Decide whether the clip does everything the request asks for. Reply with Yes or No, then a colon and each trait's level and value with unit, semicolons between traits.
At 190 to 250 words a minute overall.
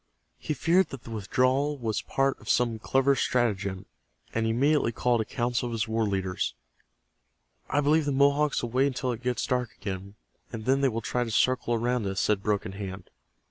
Yes: average, 195 wpm